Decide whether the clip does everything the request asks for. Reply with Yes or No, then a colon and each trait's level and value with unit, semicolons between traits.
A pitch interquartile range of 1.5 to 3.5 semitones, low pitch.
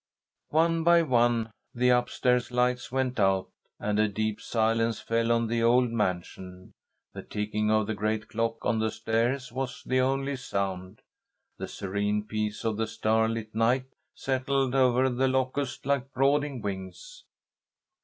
Yes: average, 3.2 semitones; low, 115 Hz